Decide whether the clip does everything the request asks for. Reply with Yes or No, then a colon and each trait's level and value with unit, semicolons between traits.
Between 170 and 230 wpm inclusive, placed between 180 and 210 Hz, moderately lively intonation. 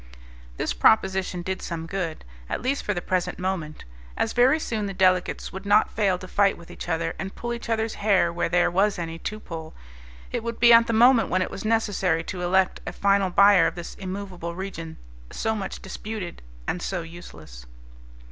Yes: average, 195 wpm; high, 190 Hz; average, 3.5 semitones